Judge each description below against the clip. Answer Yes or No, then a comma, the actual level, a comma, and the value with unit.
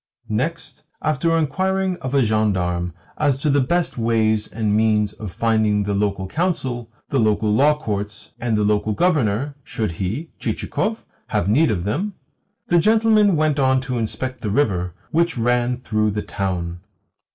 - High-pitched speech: No, low, 115 Hz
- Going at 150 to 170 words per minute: Yes, average, 160 wpm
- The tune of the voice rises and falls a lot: Yes, wide, 6.2 semitones